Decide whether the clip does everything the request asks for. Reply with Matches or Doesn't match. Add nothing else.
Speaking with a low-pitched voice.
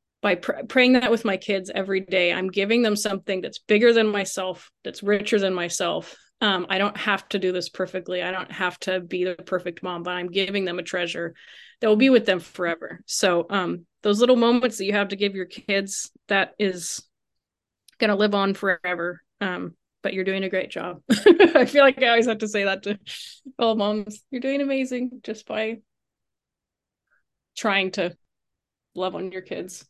Doesn't match